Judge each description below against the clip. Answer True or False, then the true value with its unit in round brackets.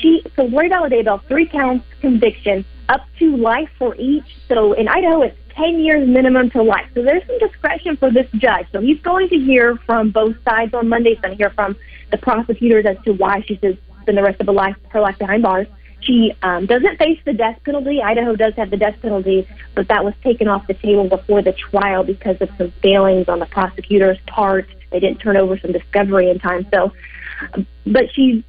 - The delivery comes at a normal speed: False (220 wpm)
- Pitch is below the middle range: False (220 Hz)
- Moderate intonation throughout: True (4.7 semitones)